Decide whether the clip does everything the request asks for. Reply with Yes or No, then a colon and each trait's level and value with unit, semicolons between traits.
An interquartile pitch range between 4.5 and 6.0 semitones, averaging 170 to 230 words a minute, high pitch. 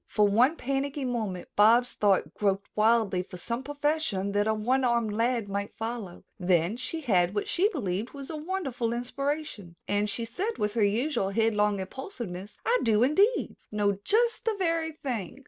Yes: wide, 5.6 semitones; average, 175 wpm; high, 230 Hz